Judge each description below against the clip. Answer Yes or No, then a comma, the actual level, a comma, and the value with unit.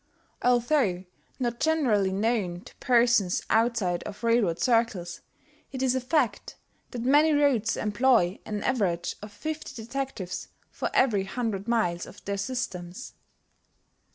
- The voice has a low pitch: No, high, 230 Hz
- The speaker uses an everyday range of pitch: Yes, average, 4.6 semitones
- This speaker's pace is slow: Yes, slow, 125 wpm